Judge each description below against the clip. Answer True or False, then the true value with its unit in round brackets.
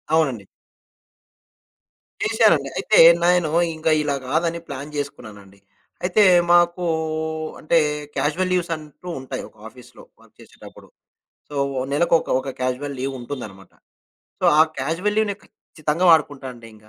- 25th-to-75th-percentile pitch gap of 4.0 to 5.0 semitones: True (4.5 semitones)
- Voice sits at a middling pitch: True (150 Hz)